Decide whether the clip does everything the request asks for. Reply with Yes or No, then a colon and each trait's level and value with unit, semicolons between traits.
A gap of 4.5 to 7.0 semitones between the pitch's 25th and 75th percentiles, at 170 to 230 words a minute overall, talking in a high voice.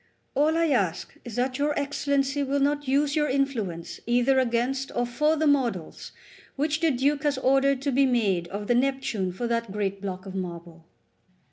Yes: wide, 5.5 semitones; average, 180 wpm; very high, 260 Hz